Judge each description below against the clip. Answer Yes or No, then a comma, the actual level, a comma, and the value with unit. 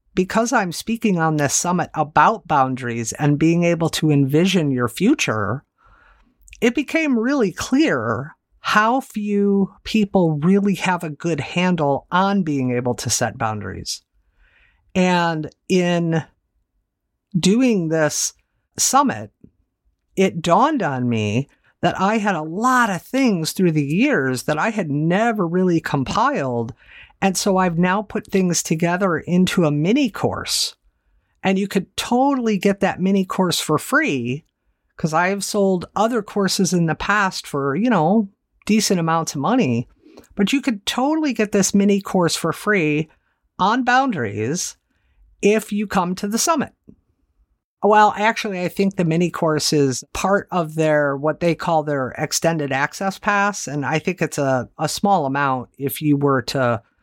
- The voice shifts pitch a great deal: Yes, wide, 5.7 semitones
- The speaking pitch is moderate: Yes, medium, 175 Hz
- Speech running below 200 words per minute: Yes, average, 150 wpm